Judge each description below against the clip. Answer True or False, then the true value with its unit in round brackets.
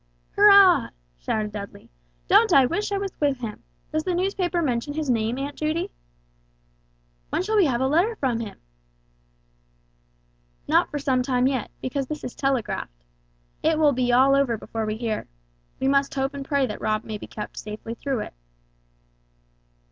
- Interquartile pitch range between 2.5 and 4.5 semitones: False (4.9 semitones)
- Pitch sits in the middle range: False (270 Hz)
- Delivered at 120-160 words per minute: False (170 wpm)